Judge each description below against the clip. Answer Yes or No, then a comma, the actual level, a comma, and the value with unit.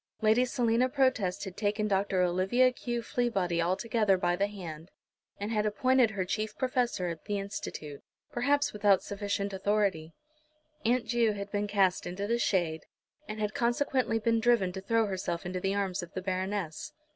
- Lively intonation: No, average, 3.7 semitones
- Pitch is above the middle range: Yes, high, 205 Hz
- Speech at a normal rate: Yes, average, 170 wpm